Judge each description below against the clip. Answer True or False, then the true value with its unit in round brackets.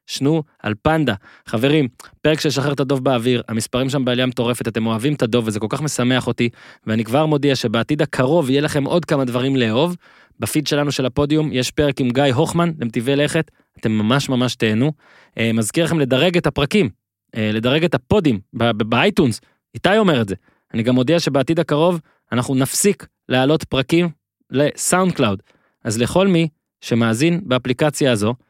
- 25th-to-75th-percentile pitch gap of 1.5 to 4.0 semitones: False (4.4 semitones)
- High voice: False (135 Hz)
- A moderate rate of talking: False (170 wpm)